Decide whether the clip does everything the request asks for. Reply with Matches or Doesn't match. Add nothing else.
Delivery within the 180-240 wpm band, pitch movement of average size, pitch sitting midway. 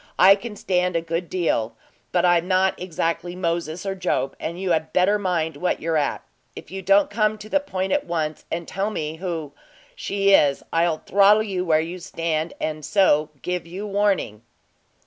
Matches